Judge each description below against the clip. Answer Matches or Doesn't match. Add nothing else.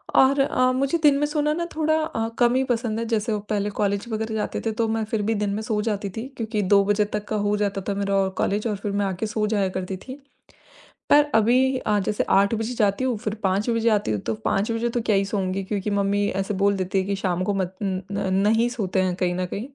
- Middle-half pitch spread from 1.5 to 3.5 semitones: Matches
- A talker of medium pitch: Doesn't match